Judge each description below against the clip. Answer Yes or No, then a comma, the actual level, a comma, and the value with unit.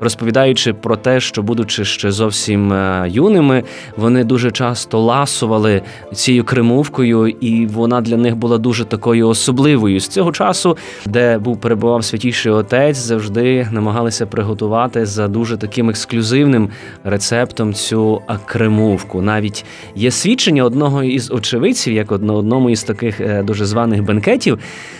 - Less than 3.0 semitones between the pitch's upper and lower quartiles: Yes, narrow, 2.4 semitones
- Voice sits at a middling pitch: No, low, 115 Hz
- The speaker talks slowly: No, average, 130 wpm